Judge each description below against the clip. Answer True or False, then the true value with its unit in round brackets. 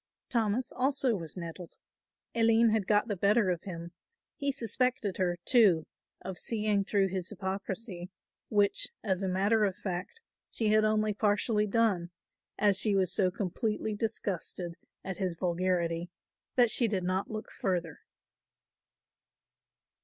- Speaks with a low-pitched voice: False (200 Hz)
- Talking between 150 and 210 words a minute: False (140 wpm)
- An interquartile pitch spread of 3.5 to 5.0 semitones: False (3.1 semitones)